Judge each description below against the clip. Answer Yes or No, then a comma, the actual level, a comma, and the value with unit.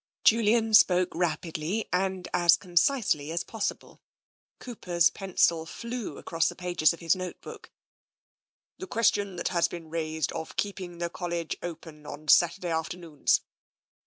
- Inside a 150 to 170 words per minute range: No, average, 140 wpm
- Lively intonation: No, average, 2.9 semitones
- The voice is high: No, medium, 175 Hz